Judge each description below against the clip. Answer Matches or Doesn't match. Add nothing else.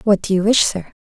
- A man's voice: Doesn't match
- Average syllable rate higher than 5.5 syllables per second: Matches